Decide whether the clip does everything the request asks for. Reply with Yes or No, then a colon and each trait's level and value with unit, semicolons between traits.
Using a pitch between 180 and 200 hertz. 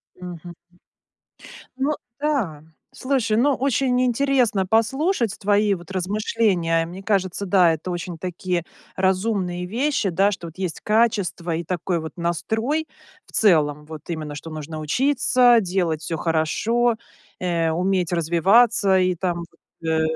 Yes: medium, 185 Hz